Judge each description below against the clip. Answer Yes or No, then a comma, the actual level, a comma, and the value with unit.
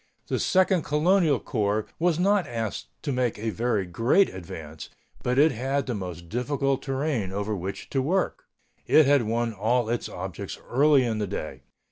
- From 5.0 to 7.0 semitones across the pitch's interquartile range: Yes, wide, 5.6 semitones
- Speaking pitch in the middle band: No, low, 120 Hz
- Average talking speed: Yes, average, 170 wpm